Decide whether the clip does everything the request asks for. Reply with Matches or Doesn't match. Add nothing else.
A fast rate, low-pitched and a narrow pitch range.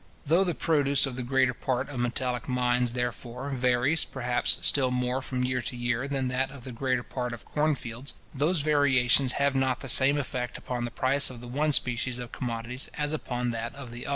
Matches